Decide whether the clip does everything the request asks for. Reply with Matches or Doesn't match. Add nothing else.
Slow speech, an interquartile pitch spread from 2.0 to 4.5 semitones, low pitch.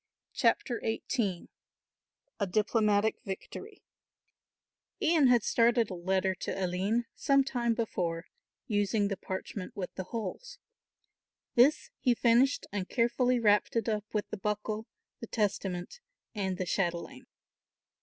Doesn't match